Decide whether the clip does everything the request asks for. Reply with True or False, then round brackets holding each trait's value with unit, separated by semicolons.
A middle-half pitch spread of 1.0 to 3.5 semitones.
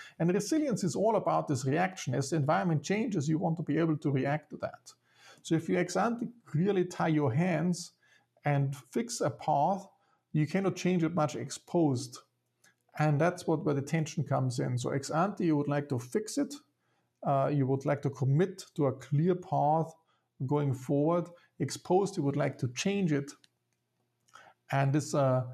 False (4.1 semitones)